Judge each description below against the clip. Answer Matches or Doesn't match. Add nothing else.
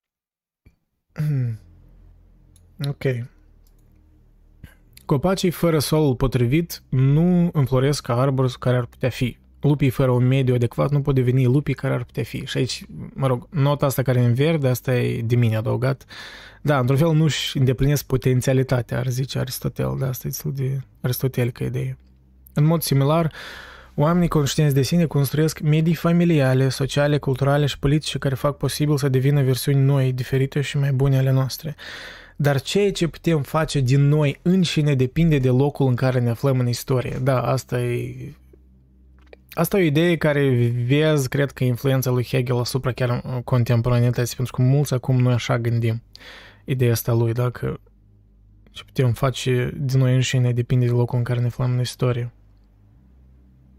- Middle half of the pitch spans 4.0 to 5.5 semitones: Doesn't match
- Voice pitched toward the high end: Doesn't match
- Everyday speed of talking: Matches